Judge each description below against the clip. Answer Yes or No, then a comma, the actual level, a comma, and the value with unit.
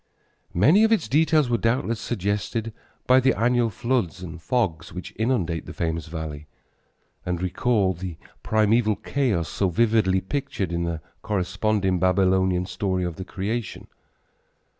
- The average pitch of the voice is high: No, low, 100 Hz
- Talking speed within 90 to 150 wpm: Yes, average, 140 wpm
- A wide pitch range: No, average, 4.8 semitones